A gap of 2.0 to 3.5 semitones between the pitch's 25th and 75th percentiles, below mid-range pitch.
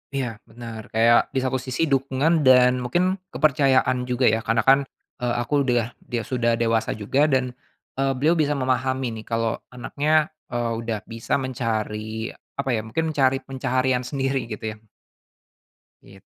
Yes: average, 2.8 semitones; low, 125 Hz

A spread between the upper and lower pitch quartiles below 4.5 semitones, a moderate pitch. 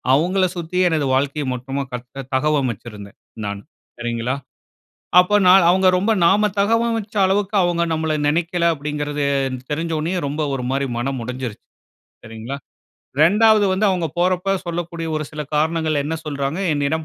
No: average, 4.8 semitones; medium, 155 Hz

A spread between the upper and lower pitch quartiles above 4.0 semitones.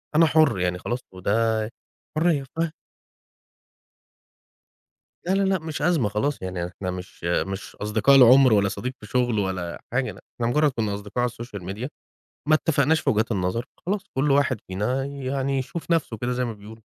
Yes: wide, 5.5 semitones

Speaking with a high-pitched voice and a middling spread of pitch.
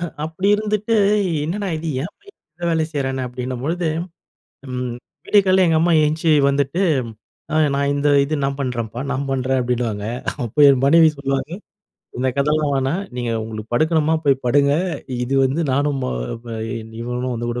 No: medium, 140 Hz; average, 4.2 semitones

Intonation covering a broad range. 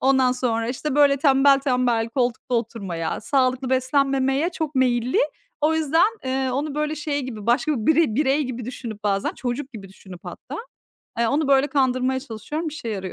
No: average, 3.3 semitones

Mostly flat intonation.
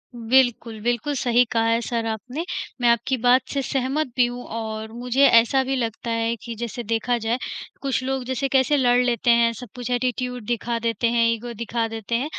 Yes: narrow, 1.8 semitones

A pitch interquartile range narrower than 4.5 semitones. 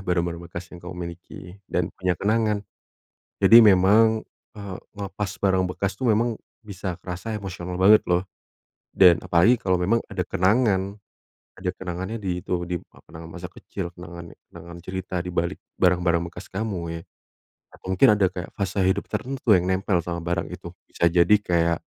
Yes: narrow, 2.5 semitones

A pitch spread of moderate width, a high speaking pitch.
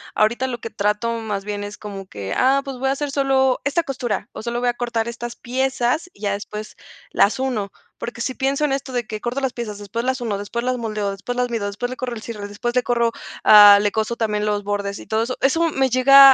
Yes: average, 3.7 semitones; high, 235 Hz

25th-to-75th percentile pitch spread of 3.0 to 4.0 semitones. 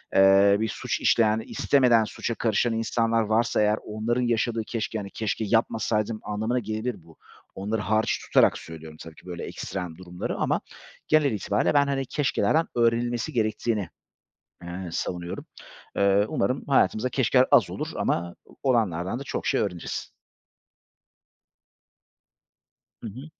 Yes: average, 3.3 semitones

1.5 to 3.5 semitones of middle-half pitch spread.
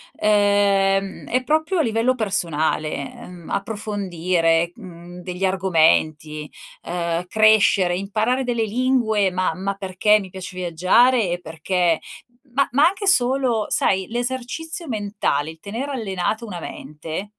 No: average, 4.7 semitones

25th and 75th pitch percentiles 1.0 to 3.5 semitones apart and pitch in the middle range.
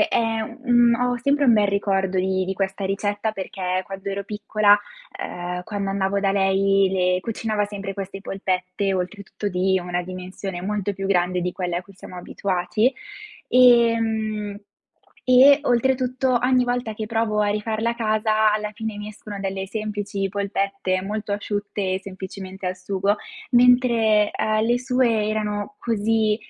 No: narrow, 2.6 semitones; high, 205 Hz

